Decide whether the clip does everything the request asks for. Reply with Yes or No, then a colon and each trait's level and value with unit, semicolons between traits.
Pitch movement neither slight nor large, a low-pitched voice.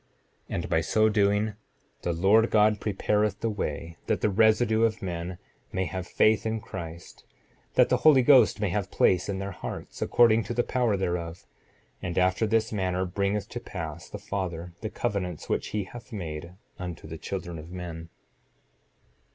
Yes: average, 3.7 semitones; low, 100 Hz